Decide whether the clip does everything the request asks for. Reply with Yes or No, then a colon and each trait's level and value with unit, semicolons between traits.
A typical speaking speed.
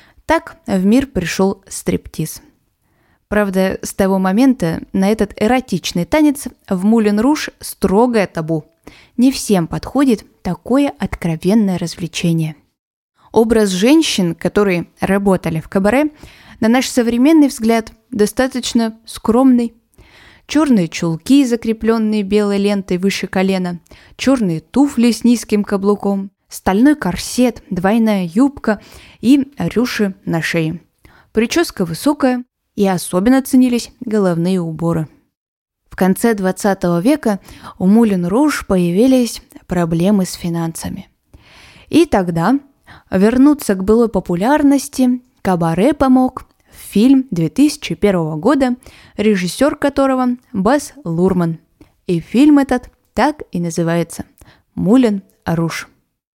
No: slow, 105 wpm